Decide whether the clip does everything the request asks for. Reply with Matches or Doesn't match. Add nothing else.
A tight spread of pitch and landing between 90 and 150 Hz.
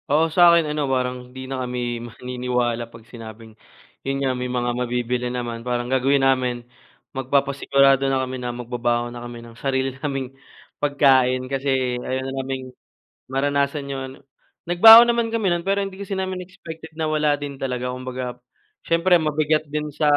Doesn't match